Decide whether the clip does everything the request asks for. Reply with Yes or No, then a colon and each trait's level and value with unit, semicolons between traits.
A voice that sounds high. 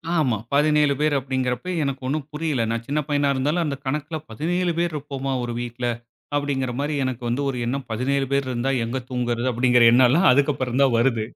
No: low, 135 Hz